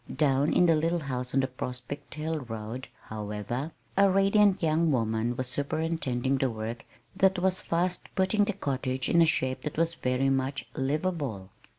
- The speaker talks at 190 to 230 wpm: No, average, 170 wpm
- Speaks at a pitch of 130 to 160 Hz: Yes, medium, 140 Hz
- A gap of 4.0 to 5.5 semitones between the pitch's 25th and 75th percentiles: Yes, average, 4.8 semitones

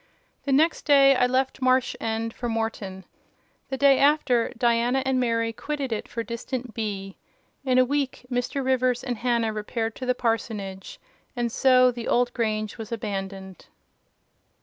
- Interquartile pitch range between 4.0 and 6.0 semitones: No, narrow, 2.6 semitones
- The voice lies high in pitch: Yes, high, 240 Hz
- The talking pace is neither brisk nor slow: Yes, average, 155 wpm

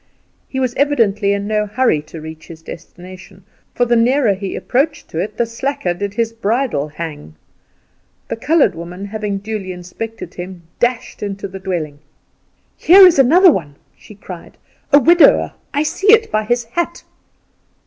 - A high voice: Yes, high, 210 Hz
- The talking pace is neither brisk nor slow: Yes, average, 160 wpm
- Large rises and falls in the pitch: Yes, wide, 5.9 semitones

